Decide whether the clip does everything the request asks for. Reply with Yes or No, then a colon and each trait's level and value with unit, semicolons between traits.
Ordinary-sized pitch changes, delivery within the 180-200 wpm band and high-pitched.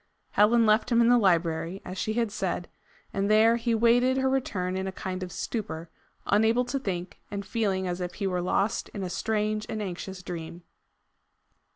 Yes: average, 3.8 semitones; average, 190 wpm; high, 200 Hz